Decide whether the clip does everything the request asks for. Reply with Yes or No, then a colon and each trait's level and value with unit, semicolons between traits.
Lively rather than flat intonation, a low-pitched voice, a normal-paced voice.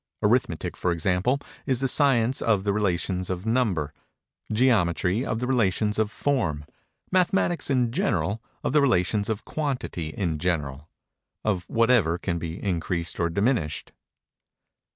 No: wide, 6.3 semitones; low, 105 Hz; slow, 125 wpm